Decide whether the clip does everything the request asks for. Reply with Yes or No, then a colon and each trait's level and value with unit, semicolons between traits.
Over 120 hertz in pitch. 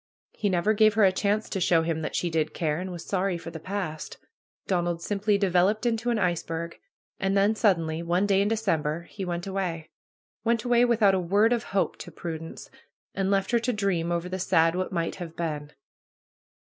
Yes: medium, 185 Hz